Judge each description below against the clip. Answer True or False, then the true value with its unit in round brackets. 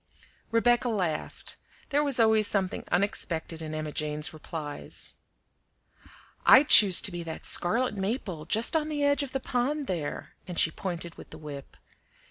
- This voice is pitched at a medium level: False (195 Hz)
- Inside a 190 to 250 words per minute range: False (155 wpm)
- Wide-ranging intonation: True (7.4 semitones)